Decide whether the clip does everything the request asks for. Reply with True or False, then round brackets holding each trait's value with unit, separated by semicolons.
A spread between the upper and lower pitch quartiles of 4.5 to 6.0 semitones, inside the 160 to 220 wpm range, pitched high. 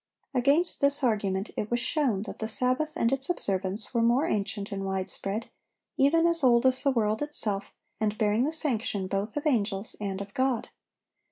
True (5.1 semitones; 180 wpm; 230 Hz)